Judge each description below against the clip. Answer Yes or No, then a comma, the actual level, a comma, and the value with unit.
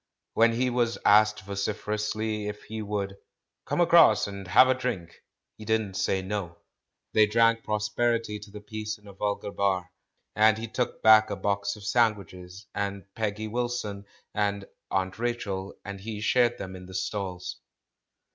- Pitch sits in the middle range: No, low, 105 Hz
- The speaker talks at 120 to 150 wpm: No, average, 165 wpm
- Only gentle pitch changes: Yes, narrow, 2.0 semitones